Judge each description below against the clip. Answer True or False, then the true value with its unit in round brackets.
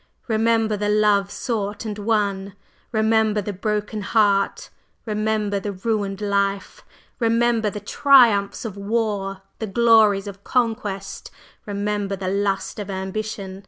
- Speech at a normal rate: False (125 wpm)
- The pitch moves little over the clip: True (1.8 semitones)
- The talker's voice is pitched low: False (210 Hz)